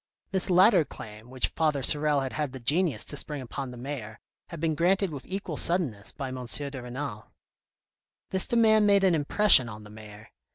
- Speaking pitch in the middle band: Yes, medium, 145 Hz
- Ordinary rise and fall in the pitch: No, wide, 6.2 semitones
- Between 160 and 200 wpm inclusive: Yes, average, 190 wpm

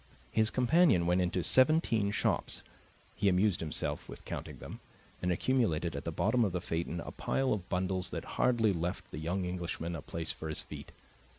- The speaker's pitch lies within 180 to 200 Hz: No, very low, 90 Hz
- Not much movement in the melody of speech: No, average, 4.5 semitones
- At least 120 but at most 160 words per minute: No, average, 185 wpm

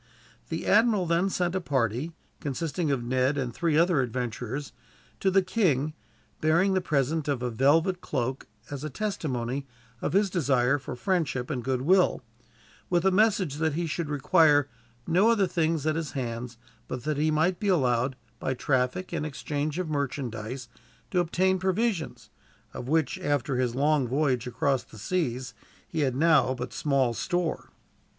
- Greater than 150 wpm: Yes, average, 160 wpm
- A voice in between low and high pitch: Yes, medium, 150 Hz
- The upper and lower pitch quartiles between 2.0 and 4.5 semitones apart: No, average, 5.2 semitones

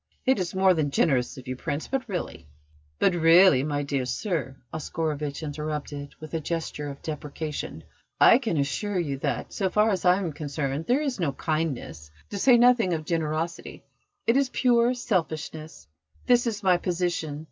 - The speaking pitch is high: No, medium, 160 Hz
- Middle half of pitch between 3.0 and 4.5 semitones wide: No, average, 5.0 semitones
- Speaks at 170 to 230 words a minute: Yes, average, 175 wpm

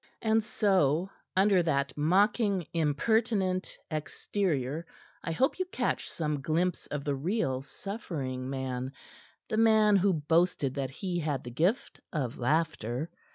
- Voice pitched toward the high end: No, medium, 165 Hz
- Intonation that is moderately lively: No, wide, 6.2 semitones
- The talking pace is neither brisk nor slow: No, slow, 130 wpm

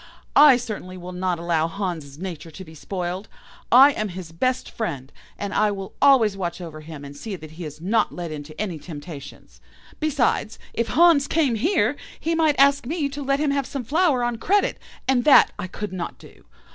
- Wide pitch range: Yes, wide, 8.4 semitones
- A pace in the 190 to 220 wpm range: Yes, average, 195 wpm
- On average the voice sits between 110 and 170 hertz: No, high, 200 Hz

